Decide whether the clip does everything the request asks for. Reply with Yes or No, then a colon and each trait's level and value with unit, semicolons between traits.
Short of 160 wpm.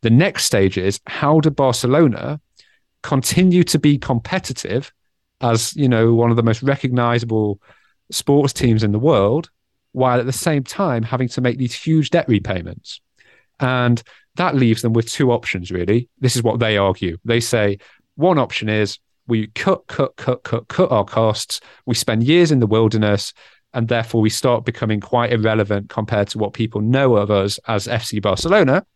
No: average, 175 wpm